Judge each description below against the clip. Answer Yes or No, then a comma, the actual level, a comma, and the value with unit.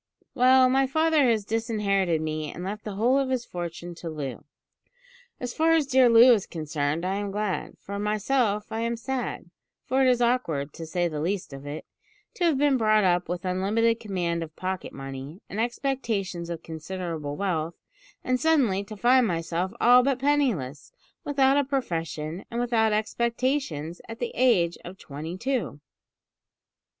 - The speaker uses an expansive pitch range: Yes, wide, 6.7 semitones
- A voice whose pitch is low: No, high, 205 Hz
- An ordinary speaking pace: Yes, average, 170 wpm